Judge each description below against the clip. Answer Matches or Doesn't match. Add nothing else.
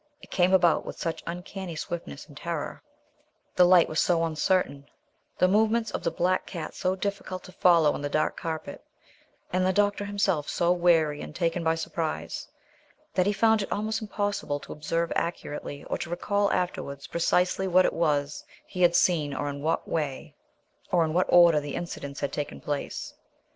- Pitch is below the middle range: Doesn't match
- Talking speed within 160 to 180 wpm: Matches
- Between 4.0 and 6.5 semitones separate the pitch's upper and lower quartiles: Doesn't match